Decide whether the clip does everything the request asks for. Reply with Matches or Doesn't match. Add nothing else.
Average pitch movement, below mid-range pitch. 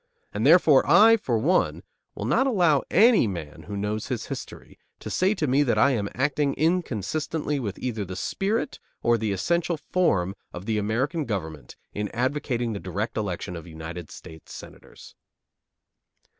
Doesn't match